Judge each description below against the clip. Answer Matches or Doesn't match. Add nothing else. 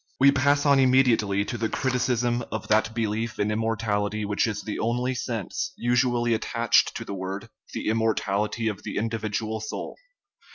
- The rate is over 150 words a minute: Matches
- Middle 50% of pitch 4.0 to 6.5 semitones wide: Doesn't match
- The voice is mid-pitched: Doesn't match